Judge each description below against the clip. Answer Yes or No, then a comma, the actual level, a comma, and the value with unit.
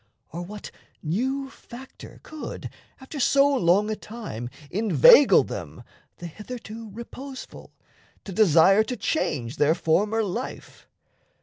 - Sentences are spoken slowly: Yes, slow, 115 wpm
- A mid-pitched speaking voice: No, high, 215 Hz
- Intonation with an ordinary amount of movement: No, wide, 6.6 semitones